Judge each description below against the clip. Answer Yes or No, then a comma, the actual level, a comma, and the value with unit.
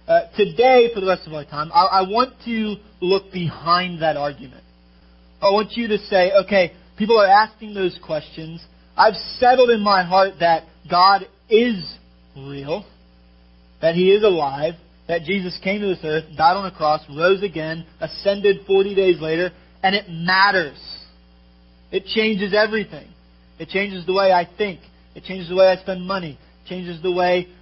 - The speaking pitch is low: No, medium, 180 Hz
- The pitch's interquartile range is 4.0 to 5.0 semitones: Yes, average, 4.4 semitones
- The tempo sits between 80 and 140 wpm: No, average, 170 wpm